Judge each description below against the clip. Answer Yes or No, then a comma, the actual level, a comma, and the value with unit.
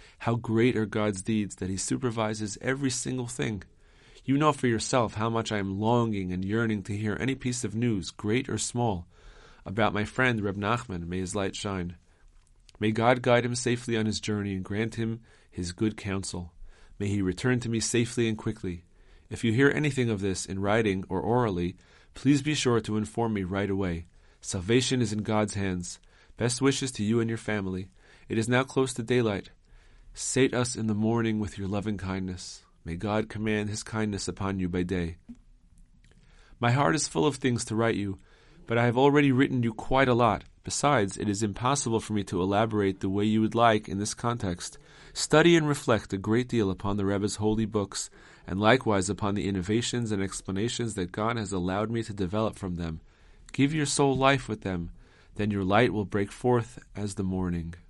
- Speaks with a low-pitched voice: Yes, low, 110 Hz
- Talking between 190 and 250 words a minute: Yes, average, 200 wpm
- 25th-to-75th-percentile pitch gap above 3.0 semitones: Yes, average, 3.7 semitones